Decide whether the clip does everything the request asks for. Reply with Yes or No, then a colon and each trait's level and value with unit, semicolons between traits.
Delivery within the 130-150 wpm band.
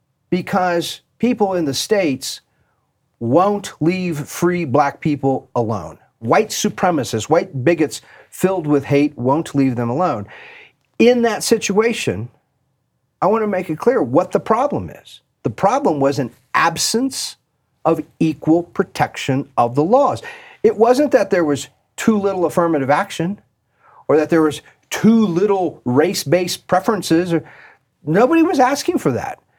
Yes: average, 140 wpm